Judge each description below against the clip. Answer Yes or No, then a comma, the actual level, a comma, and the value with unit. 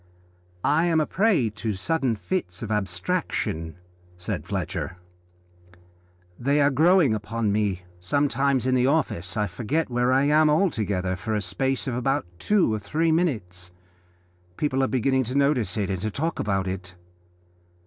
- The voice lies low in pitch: Yes, low, 125 Hz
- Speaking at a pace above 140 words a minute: Yes, average, 155 wpm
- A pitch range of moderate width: No, wide, 6.7 semitones